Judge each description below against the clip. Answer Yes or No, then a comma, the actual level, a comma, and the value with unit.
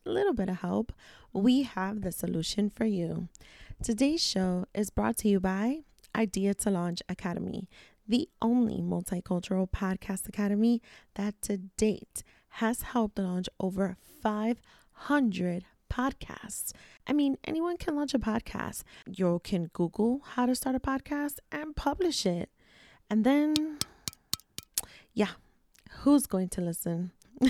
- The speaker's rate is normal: No, slow, 130 wpm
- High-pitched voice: Yes, high, 210 Hz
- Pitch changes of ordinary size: No, wide, 5.8 semitones